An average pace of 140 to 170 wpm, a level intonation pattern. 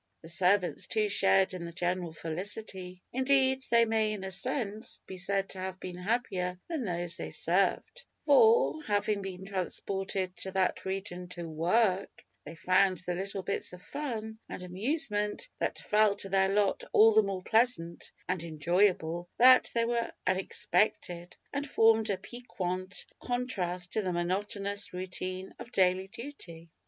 No: average, 155 wpm; average, 3.4 semitones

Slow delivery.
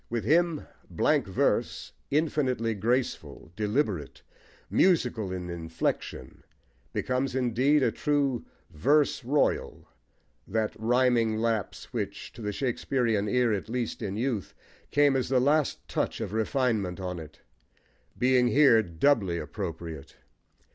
Yes: slow, 120 wpm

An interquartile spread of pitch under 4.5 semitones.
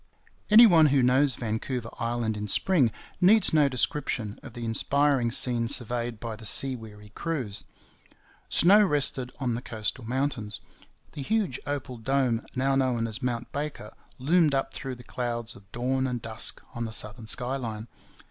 Yes: average, 3.4 semitones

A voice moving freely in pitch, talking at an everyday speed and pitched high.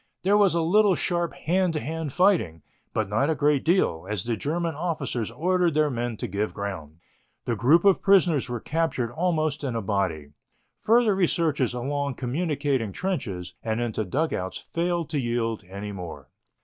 No: wide, 7.5 semitones; average, 170 wpm; medium, 145 Hz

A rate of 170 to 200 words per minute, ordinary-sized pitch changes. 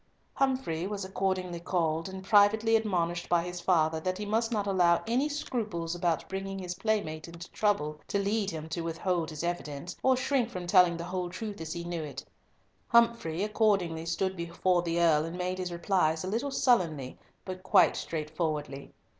Yes: average, 180 wpm; average, 3.5 semitones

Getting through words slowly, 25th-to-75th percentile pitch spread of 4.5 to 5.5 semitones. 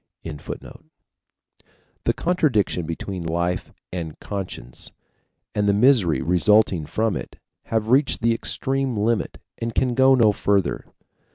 Yes: slow, 120 wpm; average, 5.0 semitones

